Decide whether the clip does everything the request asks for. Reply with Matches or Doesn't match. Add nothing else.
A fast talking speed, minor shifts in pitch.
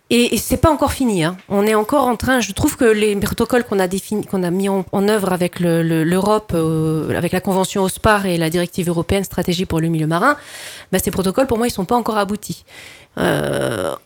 Doesn't match